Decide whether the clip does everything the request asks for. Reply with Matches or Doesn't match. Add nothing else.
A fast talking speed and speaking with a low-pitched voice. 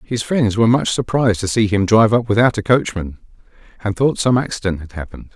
Matches